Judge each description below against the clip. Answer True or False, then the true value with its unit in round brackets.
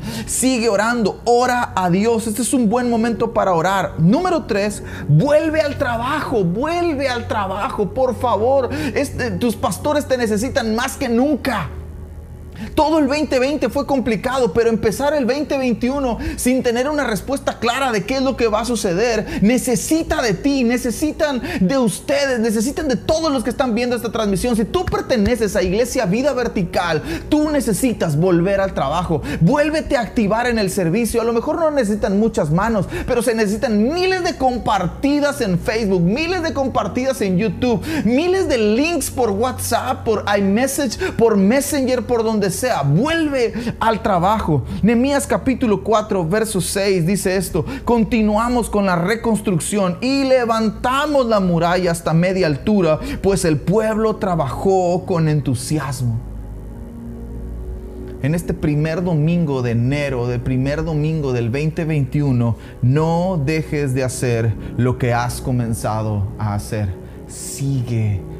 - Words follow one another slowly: False (145 wpm)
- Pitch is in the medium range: False (220 Hz)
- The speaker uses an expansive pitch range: True (7.5 semitones)